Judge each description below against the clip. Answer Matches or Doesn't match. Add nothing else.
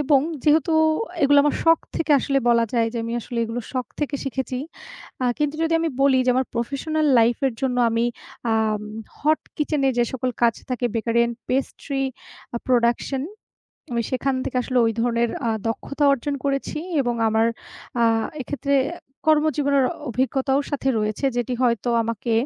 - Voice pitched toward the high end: Matches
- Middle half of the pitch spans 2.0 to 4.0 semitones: Matches